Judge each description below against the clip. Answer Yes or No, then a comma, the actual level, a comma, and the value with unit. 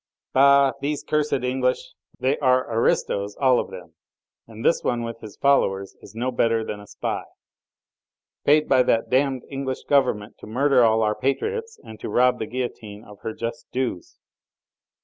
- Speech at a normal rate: Yes, average, 170 wpm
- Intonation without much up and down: No, average, 3.6 semitones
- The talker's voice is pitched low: Yes, low, 125 Hz